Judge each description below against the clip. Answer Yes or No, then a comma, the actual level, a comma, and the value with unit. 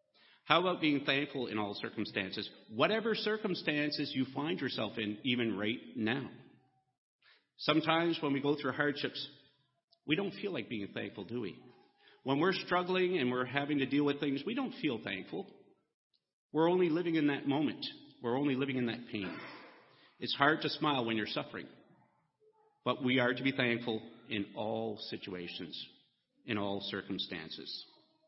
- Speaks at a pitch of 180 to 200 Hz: No, medium, 140 Hz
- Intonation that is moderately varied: No, wide, 6.2 semitones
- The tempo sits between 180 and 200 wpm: No, average, 160 wpm